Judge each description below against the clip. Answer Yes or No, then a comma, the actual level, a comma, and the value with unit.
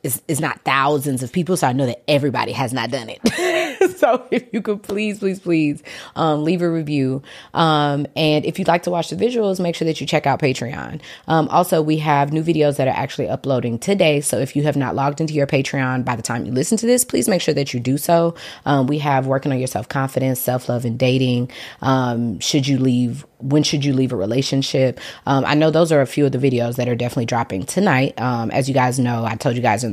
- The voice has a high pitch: No, medium, 140 Hz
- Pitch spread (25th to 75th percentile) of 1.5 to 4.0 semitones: Yes, average, 3.5 semitones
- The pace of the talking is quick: Yes, fast, 245 wpm